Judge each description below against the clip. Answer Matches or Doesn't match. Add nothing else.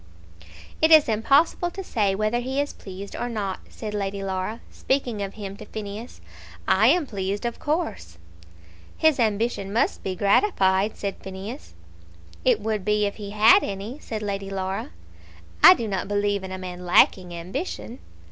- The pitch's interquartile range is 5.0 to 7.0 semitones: Doesn't match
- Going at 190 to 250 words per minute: Doesn't match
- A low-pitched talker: Doesn't match